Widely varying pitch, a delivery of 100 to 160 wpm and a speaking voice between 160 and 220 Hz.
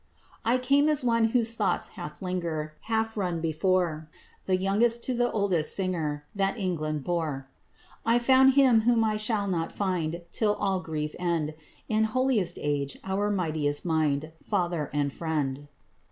Yes: wide, 6.1 semitones; average, 155 wpm; medium, 185 Hz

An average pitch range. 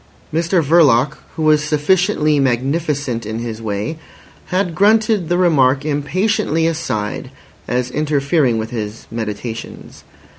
No: wide, 5.7 semitones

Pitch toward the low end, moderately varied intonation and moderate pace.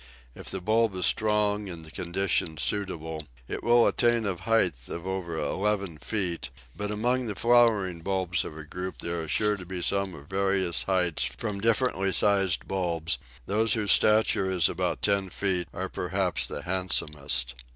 Yes: very low, 95 Hz; average, 3.4 semitones; average, 170 wpm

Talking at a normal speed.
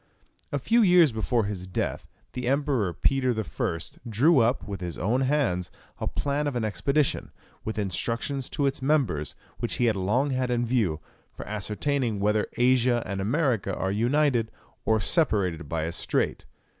Yes: average, 165 wpm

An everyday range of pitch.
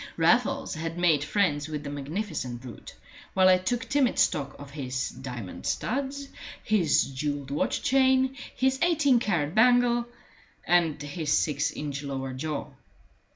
No: wide, 8.9 semitones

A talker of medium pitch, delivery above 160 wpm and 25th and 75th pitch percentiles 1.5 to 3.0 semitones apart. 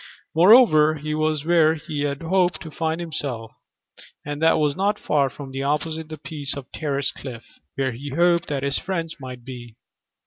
Yes: medium, 150 Hz; average, 180 wpm; average, 2.7 semitones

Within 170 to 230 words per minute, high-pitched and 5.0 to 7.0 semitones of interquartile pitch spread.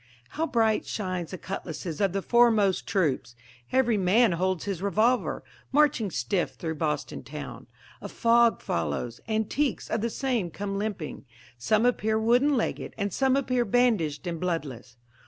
No: average, 150 wpm; high, 205 Hz; wide, 5.6 semitones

